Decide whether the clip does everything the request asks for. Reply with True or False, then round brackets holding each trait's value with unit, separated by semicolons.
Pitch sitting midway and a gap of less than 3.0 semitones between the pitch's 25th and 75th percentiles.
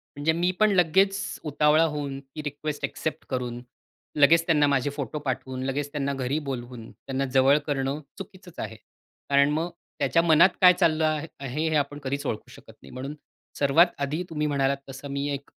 True (145 Hz; 2.6 semitones)